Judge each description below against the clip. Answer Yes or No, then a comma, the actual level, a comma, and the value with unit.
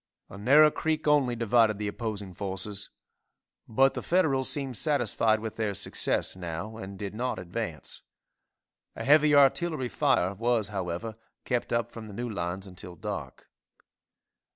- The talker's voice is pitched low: Yes, low, 110 Hz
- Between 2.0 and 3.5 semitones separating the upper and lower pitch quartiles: No, average, 5.0 semitones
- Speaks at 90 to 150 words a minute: Yes, average, 145 wpm